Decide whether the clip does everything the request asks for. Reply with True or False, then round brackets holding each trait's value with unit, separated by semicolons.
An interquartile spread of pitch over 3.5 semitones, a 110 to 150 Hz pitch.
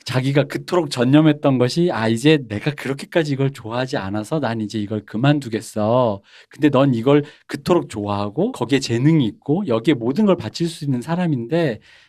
True (5.2 semitones; 135 Hz)